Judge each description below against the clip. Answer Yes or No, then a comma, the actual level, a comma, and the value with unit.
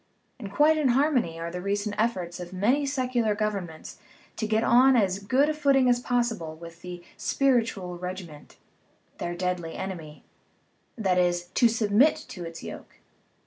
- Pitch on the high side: Yes, high, 205 Hz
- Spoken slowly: No, average, 150 wpm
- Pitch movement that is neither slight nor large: No, wide, 5.7 semitones